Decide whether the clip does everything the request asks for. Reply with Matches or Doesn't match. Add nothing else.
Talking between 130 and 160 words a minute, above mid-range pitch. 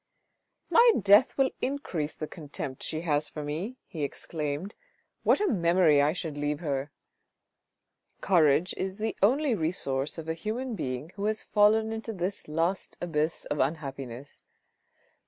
Doesn't match